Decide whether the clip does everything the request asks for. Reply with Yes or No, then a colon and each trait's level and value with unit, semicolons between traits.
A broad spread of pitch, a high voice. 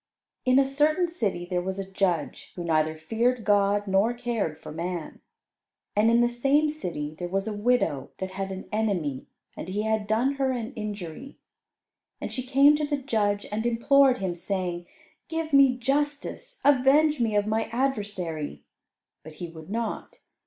Yes: wide, 6.2 semitones; high, 215 Hz